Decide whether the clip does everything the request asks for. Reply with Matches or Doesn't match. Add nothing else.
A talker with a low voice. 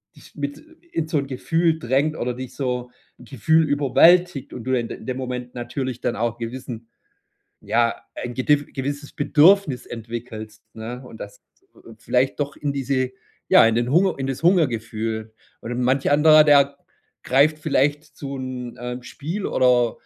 Matches